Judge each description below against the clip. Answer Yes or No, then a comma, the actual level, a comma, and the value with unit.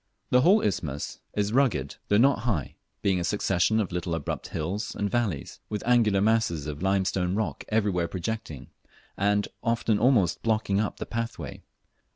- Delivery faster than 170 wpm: No, average, 165 wpm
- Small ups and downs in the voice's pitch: No, average, 4.1 semitones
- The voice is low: Yes, low, 100 Hz